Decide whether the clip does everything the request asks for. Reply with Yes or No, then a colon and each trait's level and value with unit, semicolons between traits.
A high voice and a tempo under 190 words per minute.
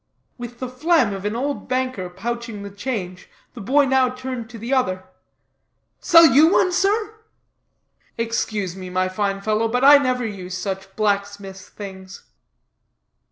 Yes: high, 225 Hz; average, 150 wpm